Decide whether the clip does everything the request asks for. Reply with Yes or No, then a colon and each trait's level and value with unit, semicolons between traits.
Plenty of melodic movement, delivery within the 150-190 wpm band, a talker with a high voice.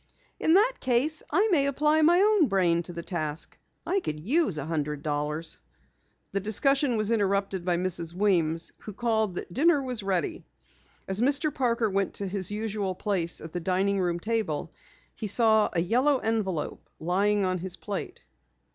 Yes: wide, 6.1 semitones; average, 170 wpm; high, 200 Hz